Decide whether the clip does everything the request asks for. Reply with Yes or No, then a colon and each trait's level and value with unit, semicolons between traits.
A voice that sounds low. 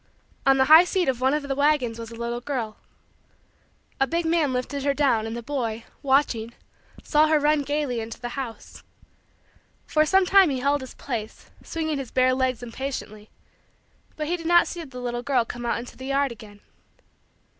No: very high, 265 Hz